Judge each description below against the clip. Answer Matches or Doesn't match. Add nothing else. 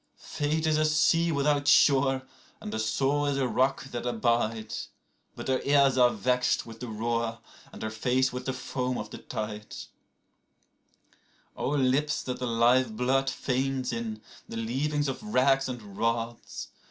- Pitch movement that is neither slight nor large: Matches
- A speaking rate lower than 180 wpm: Matches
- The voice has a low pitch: Matches